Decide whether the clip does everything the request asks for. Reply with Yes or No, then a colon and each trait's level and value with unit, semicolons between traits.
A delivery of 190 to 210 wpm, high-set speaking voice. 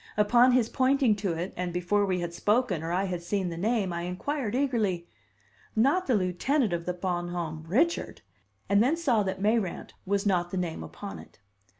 Yes: average, 195 wpm; high, 195 Hz